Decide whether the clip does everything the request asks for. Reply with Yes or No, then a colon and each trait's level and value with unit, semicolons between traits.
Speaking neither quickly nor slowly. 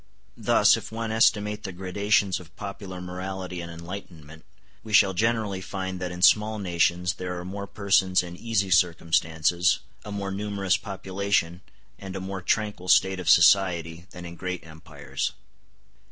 Yes: average, 155 wpm